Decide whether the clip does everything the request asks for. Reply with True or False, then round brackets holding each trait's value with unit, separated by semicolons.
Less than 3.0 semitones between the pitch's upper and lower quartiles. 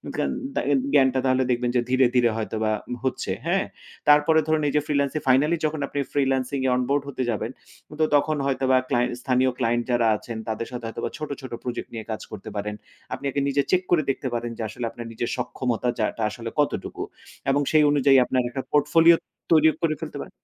False (3.4 semitones)